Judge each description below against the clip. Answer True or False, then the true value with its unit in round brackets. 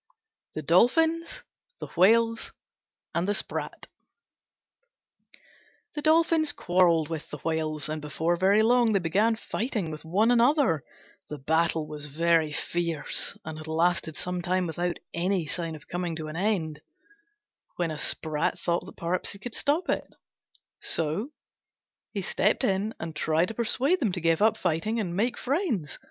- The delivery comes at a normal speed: True (155 wpm)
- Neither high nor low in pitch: True (175 Hz)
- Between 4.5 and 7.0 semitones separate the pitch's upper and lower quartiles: True (5.6 semitones)